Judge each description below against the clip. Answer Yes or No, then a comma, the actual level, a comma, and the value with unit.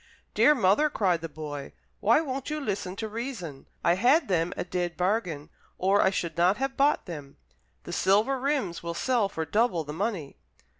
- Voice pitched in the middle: No, high, 195 Hz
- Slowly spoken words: No, average, 185 wpm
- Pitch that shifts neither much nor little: No, wide, 6.6 semitones